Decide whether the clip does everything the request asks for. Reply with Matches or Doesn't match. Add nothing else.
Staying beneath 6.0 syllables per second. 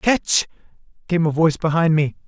Matches